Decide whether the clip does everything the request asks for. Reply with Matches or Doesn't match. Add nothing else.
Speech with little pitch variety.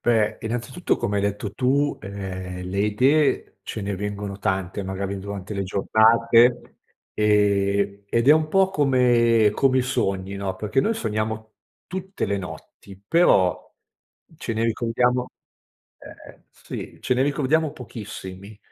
Doesn't match